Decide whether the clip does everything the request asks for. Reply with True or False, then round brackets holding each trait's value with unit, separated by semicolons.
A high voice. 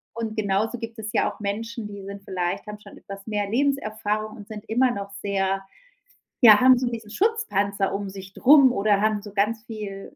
True (210 Hz)